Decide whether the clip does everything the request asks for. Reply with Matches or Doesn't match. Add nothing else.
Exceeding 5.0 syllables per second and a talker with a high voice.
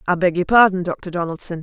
Doesn't match